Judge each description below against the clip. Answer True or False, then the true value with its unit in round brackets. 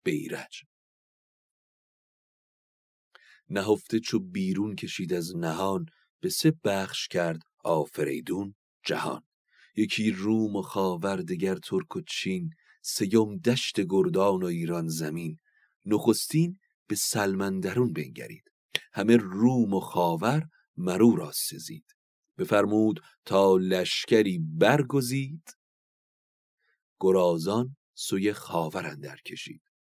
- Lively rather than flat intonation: True (6.4 semitones)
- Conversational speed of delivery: False (95 wpm)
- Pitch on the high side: False (105 Hz)